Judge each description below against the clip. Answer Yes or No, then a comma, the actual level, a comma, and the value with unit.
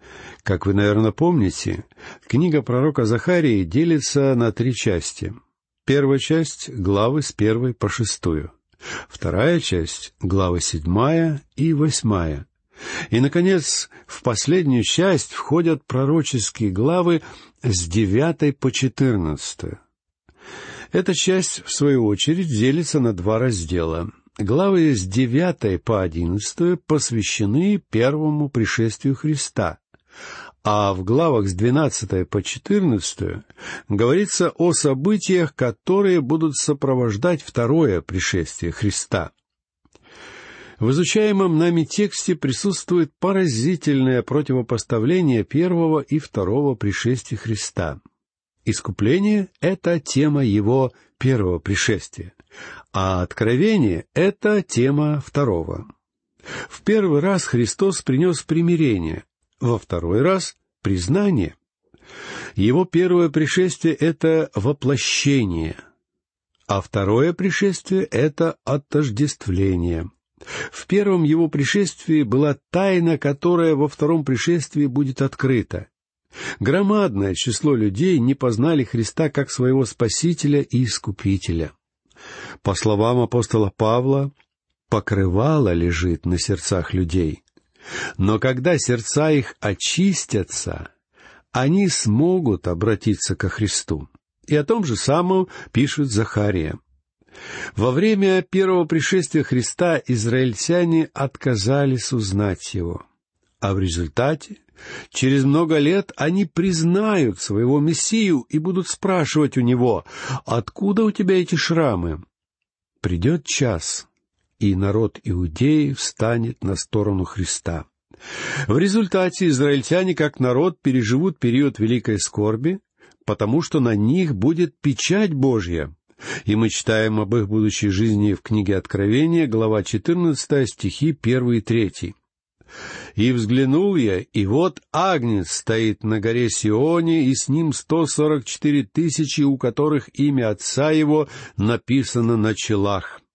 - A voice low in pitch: Yes, low, 130 Hz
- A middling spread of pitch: No, wide, 7.2 semitones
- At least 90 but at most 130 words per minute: Yes, slow, 110 wpm